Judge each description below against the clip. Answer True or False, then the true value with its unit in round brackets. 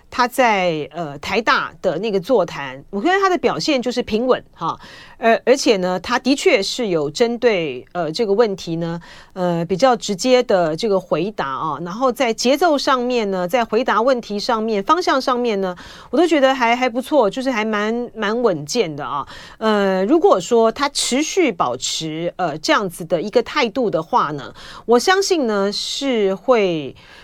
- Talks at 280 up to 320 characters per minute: False (255 characters per minute)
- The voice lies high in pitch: True (225 Hz)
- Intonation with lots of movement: True (5.8 semitones)